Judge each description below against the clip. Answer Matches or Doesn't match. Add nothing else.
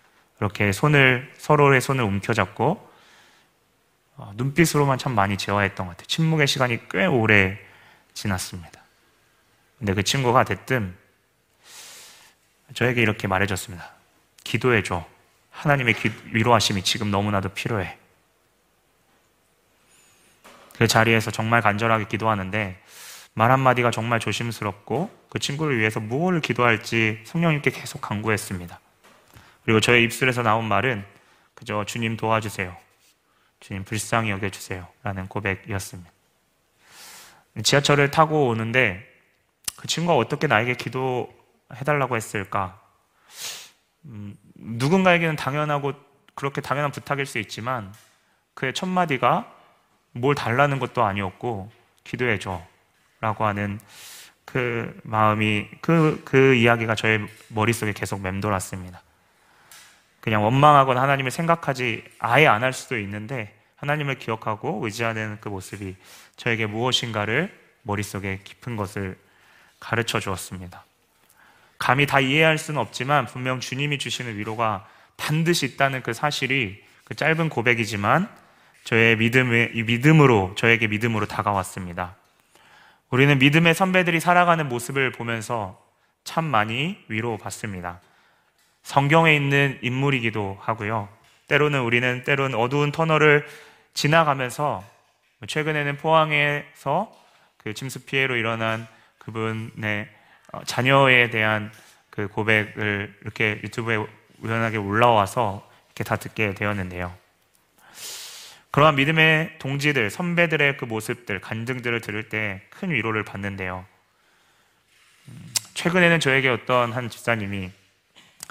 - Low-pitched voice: Matches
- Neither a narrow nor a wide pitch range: Matches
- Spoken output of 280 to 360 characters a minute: Matches